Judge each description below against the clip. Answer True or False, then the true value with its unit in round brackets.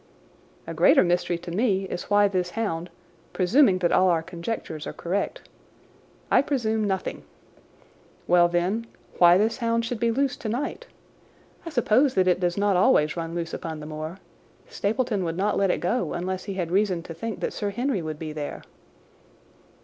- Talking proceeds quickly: False (175 wpm)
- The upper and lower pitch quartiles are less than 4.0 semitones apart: False (4.4 semitones)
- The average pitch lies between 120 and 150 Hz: False (185 Hz)